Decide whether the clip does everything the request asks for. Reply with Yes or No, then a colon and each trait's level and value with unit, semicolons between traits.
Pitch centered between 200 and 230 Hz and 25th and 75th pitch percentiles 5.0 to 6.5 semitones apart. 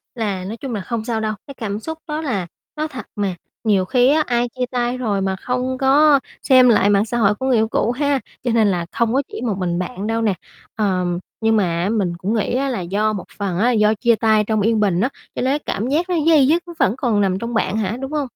No: high, 225 Hz; average, 4.2 semitones